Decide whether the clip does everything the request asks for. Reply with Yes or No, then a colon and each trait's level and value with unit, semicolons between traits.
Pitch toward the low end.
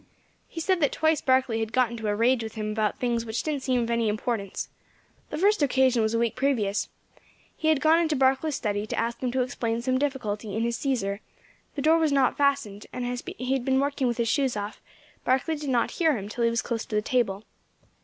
No: high, 245 Hz